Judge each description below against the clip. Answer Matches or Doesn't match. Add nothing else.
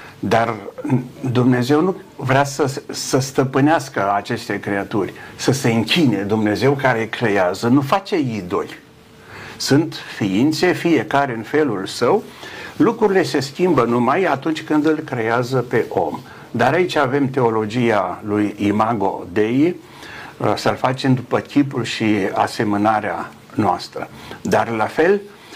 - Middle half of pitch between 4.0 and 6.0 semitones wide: Matches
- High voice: Doesn't match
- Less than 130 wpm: Matches